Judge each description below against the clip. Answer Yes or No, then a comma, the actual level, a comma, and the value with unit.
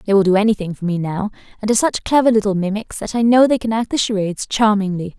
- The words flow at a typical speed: No, fast, 255 wpm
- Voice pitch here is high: Yes, high, 210 Hz